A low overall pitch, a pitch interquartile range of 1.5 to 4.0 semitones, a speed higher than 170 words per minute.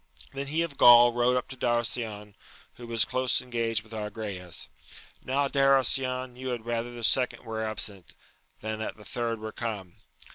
Yes: low, 120 Hz; narrow, 2.6 semitones; average, 180 wpm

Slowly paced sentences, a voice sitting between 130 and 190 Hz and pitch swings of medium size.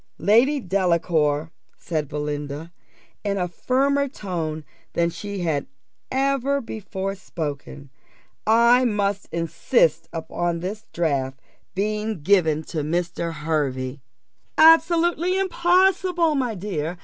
No: slow, 100 wpm; medium, 185 Hz; wide, 7.8 semitones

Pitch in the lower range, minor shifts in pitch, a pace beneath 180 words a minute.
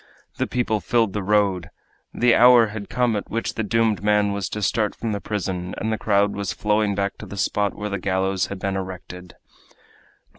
No: low, 105 Hz; narrow, 2.1 semitones; average, 200 wpm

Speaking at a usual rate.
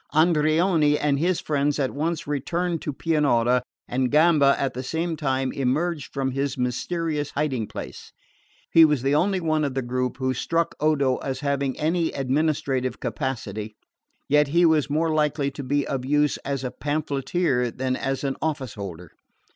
Yes: average, 165 wpm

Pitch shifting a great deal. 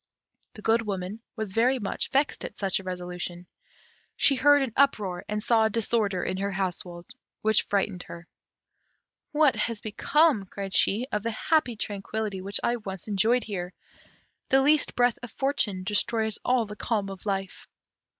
No: average, 3.6 semitones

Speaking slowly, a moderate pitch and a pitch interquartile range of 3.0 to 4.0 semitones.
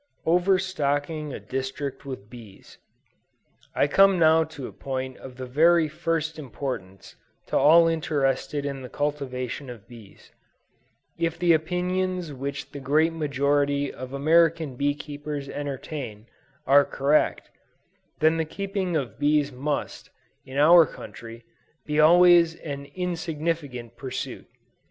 Yes: slow, 125 wpm; medium, 145 Hz; average, 3.5 semitones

